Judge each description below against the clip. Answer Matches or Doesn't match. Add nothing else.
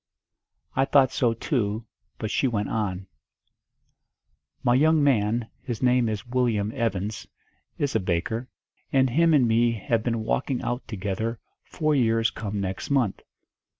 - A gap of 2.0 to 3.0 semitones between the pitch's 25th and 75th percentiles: Doesn't match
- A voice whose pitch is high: Doesn't match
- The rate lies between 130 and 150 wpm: Matches